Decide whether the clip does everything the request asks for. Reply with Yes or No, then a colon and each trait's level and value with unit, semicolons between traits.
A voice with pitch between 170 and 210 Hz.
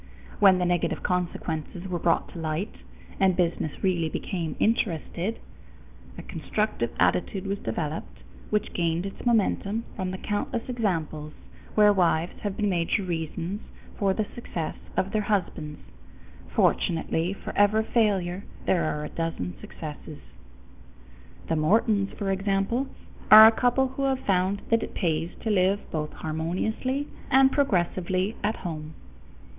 Yes: medium, 185 Hz